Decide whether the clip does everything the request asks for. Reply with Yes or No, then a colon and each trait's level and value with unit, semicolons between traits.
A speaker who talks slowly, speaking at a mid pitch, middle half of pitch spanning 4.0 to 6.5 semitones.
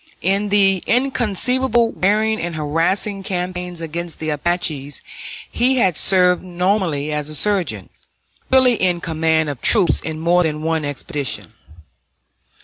Yes: slow, 130 wpm; medium, 180 Hz; average, 4.3 semitones